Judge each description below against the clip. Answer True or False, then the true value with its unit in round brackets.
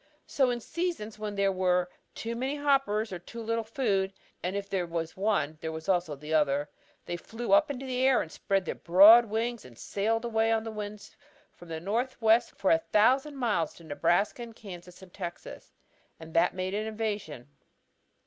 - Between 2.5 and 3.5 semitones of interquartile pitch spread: False (4.8 semitones)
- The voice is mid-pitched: False (205 Hz)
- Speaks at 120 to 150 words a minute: False (185 wpm)